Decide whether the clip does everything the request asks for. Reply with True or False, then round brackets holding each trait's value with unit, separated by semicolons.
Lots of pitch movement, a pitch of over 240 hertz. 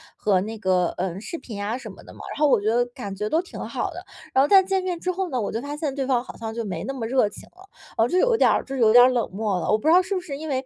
True (6.5 semitones; 250 Hz)